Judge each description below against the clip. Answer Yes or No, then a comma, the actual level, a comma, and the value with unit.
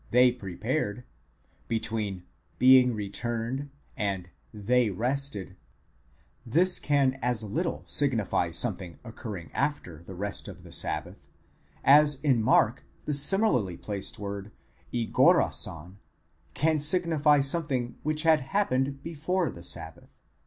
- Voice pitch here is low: Yes, low, 125 Hz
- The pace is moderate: No, slow, 110 wpm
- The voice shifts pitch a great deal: Yes, wide, 6.1 semitones